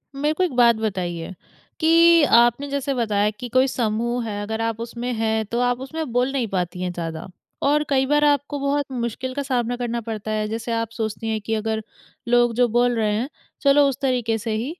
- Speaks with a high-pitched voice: Yes, high, 240 Hz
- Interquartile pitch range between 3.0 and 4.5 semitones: Yes, average, 3.6 semitones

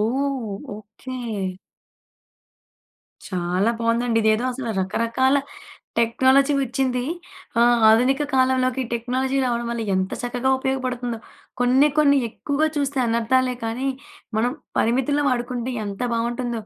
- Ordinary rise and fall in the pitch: No, narrow, 2.3 semitones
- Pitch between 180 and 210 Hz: No, high, 245 Hz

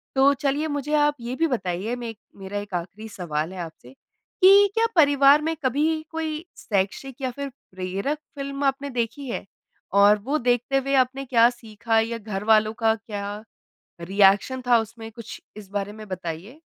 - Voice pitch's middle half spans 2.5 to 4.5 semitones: No, wide, 5.4 semitones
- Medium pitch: No, high, 235 Hz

